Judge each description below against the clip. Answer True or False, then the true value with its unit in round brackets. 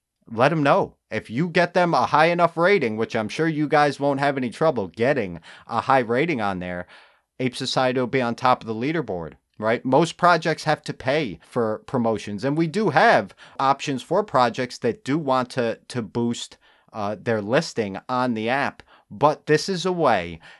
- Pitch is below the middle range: True (130 Hz)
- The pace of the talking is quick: False (195 wpm)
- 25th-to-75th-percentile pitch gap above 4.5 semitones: True (5.0 semitones)